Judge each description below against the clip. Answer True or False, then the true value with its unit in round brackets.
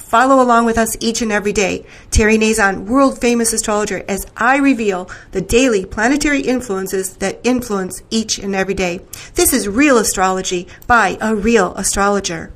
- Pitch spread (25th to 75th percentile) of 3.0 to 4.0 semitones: True (3.7 semitones)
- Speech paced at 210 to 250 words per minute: False (165 wpm)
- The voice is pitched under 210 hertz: False (220 Hz)